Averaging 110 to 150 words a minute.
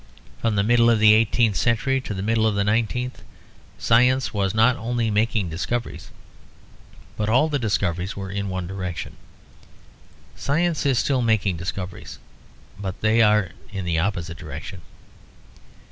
Yes: average, 145 wpm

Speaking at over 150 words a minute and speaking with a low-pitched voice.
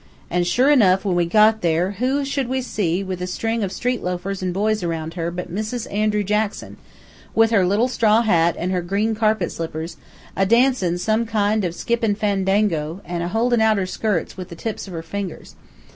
No: fast, 205 wpm; high, 200 Hz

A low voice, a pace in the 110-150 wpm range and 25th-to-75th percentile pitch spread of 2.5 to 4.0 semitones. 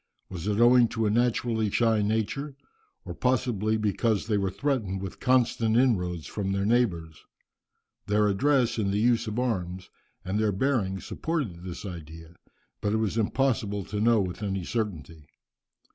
No: low, 105 Hz; average, 160 wpm; average, 3.7 semitones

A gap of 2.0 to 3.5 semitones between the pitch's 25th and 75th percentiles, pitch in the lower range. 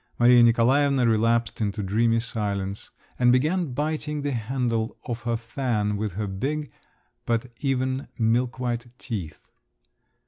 Yes: average, 2.9 semitones; low, 120 Hz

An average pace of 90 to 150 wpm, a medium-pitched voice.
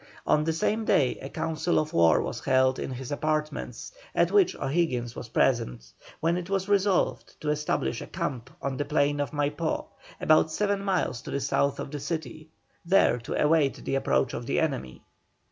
No: average, 185 wpm; medium, 150 Hz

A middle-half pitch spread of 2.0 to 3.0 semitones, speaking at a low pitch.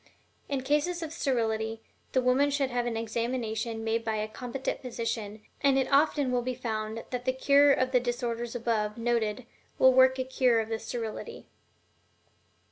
No: narrow, 2.6 semitones; high, 245 Hz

